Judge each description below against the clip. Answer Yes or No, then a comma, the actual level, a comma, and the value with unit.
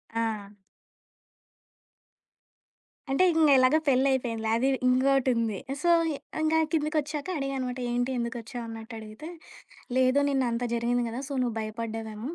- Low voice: No, very high, 250 Hz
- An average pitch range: Yes, average, 3.0 semitones